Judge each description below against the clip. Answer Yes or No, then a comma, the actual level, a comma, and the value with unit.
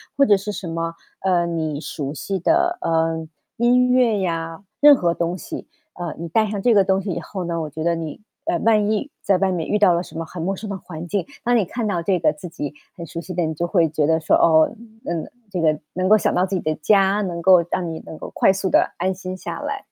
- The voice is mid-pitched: Yes, medium, 180 Hz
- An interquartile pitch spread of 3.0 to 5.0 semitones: Yes, average, 3.3 semitones